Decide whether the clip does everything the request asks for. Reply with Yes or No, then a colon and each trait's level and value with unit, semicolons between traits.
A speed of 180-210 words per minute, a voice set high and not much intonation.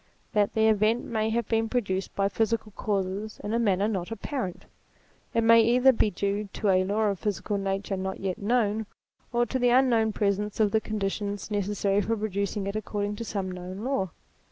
Yes: average, 200 wpm; high, 210 Hz; narrow, 2.2 semitones